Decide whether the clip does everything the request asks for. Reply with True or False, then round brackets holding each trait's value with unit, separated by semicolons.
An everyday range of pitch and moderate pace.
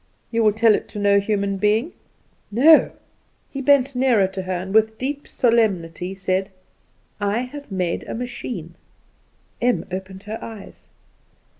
True (4.3 semitones; 145 wpm)